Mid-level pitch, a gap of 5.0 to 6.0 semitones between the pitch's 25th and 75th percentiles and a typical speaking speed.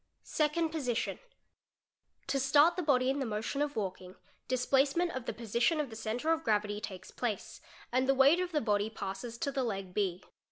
No: very high, 255 Hz; wide, 5.6 semitones; average, 190 wpm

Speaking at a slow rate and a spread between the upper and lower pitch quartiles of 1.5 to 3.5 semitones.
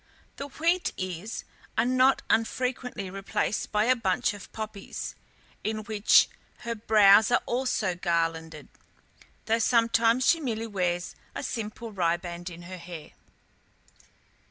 No: slow, 125 wpm; average, 4.3 semitones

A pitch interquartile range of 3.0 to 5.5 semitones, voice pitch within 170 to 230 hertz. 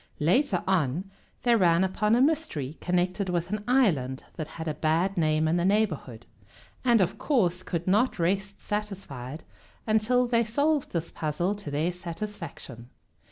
Yes: average, 4.9 semitones; medium, 185 Hz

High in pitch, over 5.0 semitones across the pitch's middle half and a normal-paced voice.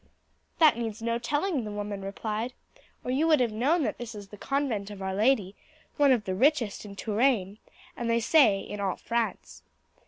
No: high, 230 Hz; average, 4.3 semitones; average, 190 wpm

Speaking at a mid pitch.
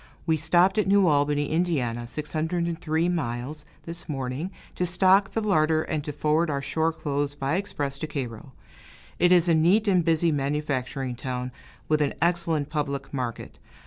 Yes: medium, 155 Hz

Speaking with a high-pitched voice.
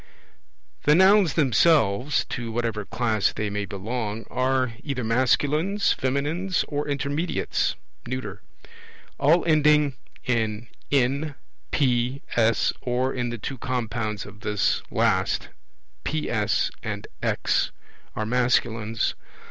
No: low, 125 Hz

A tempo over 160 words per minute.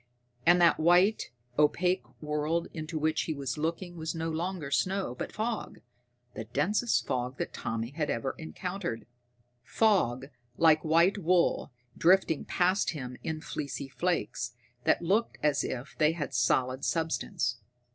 No: average, 140 wpm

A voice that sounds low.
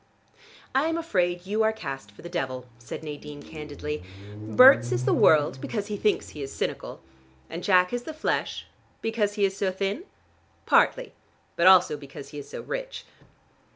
No: medium, 180 Hz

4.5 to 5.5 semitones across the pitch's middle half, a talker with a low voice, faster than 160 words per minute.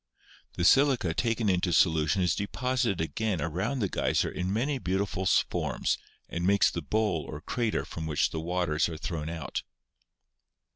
No: average, 5.0 semitones; very low, 90 Hz; average, 155 wpm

